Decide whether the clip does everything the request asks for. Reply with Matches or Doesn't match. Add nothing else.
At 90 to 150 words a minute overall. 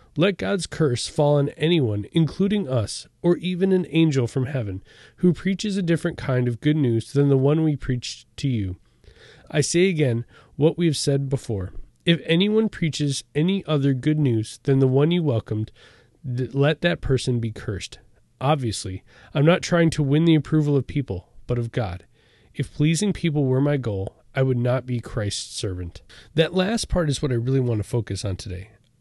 Doesn't match